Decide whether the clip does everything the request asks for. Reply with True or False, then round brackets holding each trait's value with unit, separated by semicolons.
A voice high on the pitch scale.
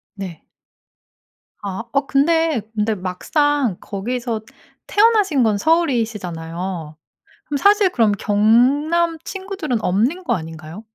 True (235 Hz)